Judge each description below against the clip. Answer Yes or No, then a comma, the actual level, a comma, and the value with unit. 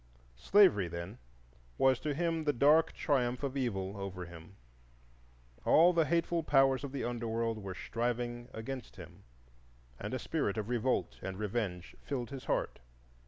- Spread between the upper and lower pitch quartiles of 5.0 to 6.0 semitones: Yes, average, 5.3 semitones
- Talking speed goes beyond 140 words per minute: Yes, average, 155 wpm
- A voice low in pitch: Yes, low, 120 Hz